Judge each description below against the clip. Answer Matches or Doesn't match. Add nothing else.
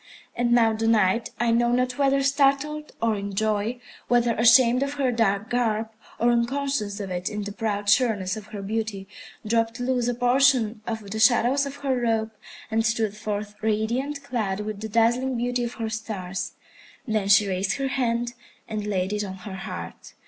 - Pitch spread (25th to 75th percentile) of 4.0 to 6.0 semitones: Doesn't match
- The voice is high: Matches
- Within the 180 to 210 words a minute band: Matches